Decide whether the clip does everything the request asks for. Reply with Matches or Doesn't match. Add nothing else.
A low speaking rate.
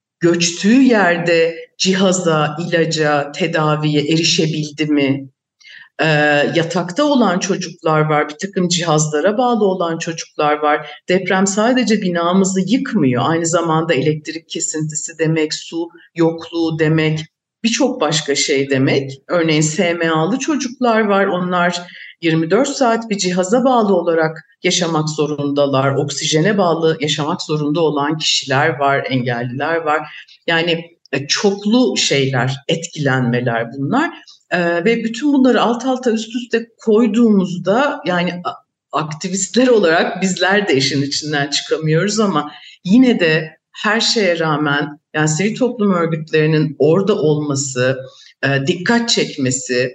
Doesn't match